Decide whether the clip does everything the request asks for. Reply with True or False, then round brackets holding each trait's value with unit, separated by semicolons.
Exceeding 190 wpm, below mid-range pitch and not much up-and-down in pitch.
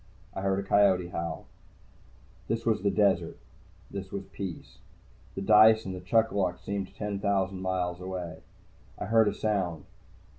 False (150 wpm; 95 Hz; 2.0 semitones)